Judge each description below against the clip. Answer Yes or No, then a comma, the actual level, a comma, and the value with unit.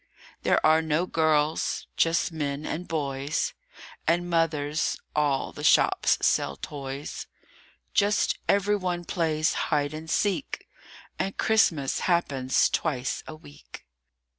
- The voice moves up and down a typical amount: Yes, average, 3.2 semitones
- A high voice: No, medium, 155 Hz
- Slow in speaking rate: Yes, slow, 115 wpm